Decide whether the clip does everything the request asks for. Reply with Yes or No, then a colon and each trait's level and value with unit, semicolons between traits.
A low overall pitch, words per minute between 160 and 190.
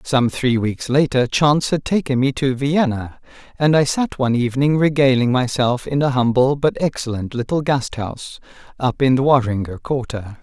Yes: low, 130 Hz; average, 165 wpm